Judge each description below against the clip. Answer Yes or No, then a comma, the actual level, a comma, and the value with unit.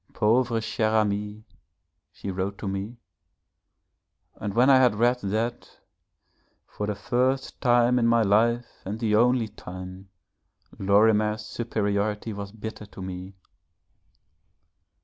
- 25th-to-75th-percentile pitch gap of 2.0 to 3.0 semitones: Yes, average, 2.7 semitones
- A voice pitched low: Yes, low, 110 Hz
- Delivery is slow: Yes, slow, 120 wpm